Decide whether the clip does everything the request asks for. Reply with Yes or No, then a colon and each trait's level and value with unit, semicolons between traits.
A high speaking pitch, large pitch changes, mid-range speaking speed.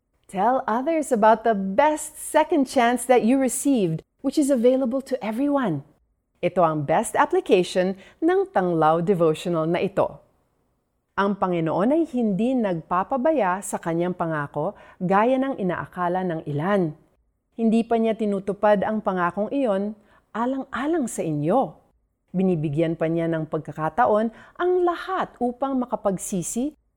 Yes: high, 205 Hz; wide, 6.9 semitones; average, 125 wpm